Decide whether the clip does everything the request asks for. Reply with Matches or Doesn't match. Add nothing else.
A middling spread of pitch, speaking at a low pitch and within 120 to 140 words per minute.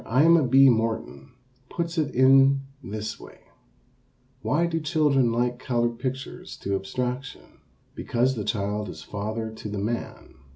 Matches